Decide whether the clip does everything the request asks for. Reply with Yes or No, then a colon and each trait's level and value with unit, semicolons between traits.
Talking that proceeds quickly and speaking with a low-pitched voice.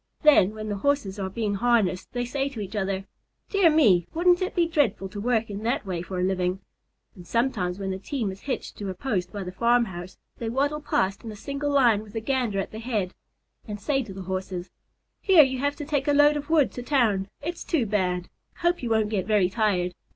No: fast, 230 wpm; high, 220 Hz